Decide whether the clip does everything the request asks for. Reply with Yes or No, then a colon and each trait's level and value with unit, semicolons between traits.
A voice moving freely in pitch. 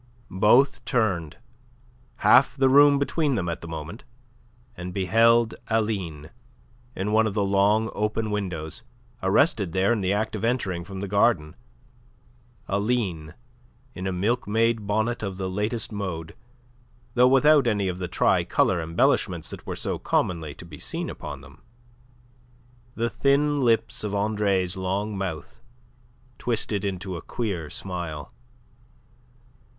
No: average, 3.9 semitones